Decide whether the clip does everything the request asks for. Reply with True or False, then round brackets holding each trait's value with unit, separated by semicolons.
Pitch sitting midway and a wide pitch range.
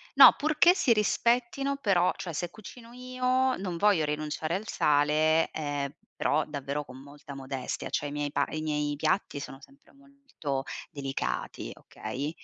True (155 Hz; 8.5 semitones)